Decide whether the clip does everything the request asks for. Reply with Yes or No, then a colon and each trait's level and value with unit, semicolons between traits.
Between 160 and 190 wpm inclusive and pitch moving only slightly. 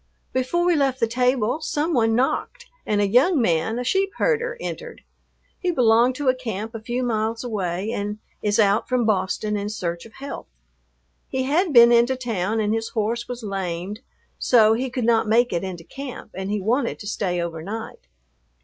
No: average, 185 wpm; average, 3.7 semitones